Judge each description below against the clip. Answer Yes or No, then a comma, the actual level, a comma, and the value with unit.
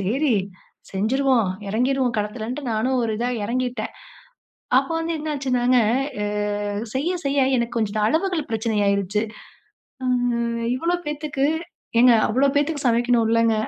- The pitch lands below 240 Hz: No, high, 245 Hz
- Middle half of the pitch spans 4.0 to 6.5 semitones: No, average, 3.6 semitones